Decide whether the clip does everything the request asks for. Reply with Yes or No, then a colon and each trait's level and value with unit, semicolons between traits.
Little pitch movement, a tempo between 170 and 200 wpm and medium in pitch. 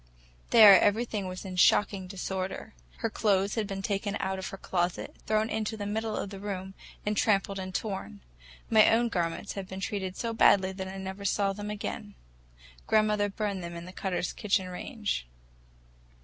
No: narrow, 2.0 semitones; average, 175 wpm; high, 200 Hz